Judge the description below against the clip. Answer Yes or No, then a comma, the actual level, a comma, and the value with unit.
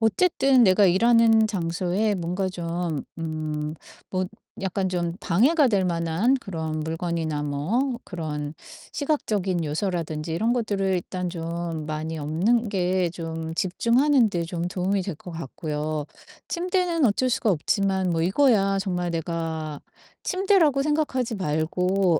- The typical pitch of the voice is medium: Yes, medium, 180 Hz